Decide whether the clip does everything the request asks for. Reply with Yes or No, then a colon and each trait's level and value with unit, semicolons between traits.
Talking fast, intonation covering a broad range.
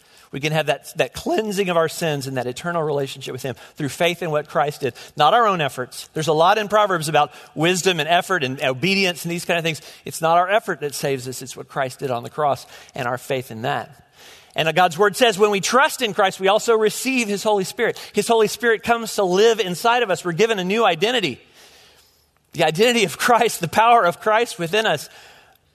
Yes: fast, 230 wpm; wide, 6.7 semitones